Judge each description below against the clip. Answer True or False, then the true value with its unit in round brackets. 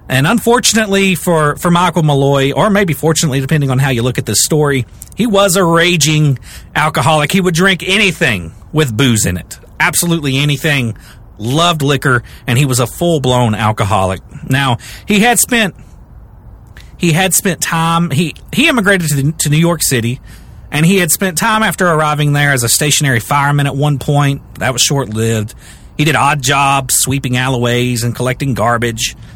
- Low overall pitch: False (145 Hz)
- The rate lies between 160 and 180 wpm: True (175 wpm)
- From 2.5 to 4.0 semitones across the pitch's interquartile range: False (5.6 semitones)